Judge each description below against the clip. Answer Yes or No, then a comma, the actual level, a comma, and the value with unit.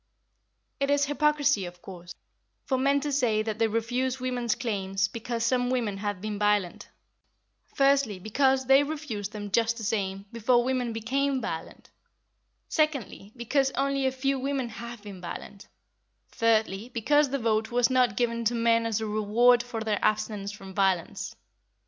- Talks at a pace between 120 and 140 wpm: No, average, 160 wpm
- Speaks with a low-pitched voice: No, high, 230 Hz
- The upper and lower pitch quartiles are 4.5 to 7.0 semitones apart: No, average, 4.0 semitones